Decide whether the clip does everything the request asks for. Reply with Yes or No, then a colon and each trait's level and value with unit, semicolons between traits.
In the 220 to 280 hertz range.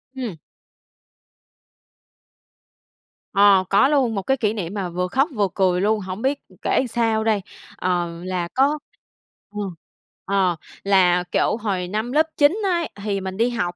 No: high, 205 Hz